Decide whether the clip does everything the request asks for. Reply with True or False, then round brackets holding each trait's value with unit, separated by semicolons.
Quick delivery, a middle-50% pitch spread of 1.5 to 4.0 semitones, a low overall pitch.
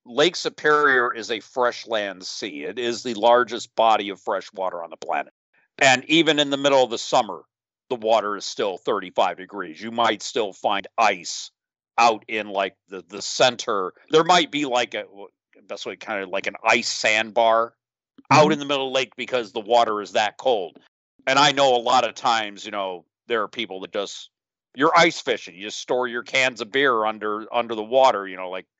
True (210 wpm; 3.6 semitones; 120 Hz)